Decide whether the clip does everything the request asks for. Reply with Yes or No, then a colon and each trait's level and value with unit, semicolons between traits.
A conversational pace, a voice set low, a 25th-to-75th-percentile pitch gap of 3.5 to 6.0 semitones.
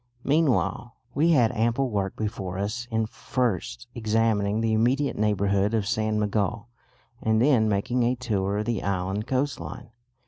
No: average, 145 wpm; low, 110 Hz; average, 3.0 semitones